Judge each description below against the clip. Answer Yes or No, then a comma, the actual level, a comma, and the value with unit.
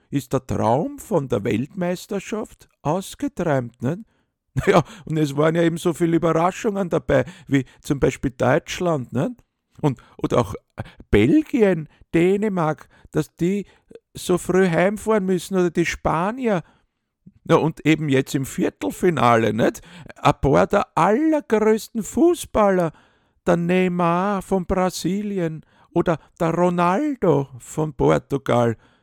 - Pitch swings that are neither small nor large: Yes, average, 4.6 semitones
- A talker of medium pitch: Yes, medium, 175 Hz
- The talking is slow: Yes, slow, 120 wpm